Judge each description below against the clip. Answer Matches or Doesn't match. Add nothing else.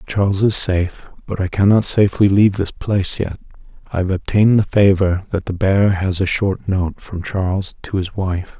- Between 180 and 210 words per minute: Matches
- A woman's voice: Doesn't match